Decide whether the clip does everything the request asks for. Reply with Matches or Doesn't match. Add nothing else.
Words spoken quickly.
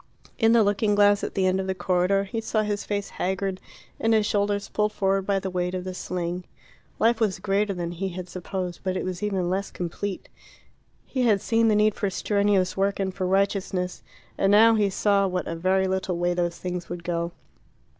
Matches